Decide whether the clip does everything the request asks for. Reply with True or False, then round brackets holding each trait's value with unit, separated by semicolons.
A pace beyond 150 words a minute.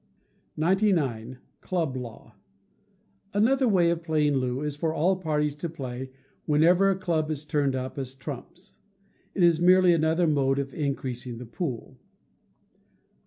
False (145 wpm)